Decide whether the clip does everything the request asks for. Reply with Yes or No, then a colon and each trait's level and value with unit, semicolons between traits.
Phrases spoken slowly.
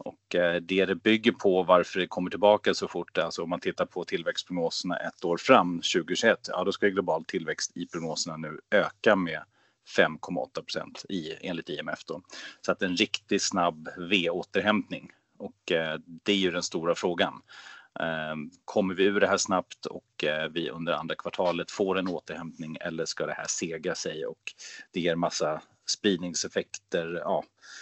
No: average, 170 wpm